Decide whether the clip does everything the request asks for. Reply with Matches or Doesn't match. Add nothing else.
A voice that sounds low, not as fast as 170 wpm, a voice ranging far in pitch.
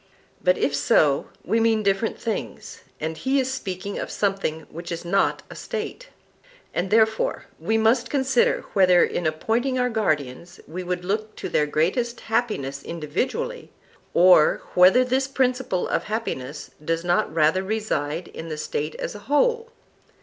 Doesn't match